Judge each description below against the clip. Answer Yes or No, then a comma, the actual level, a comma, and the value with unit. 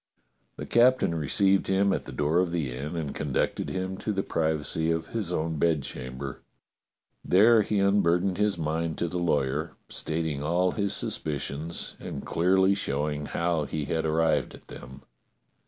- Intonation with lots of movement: No, average, 3.9 semitones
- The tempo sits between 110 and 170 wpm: Yes, average, 160 wpm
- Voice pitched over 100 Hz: No, very low, 80 Hz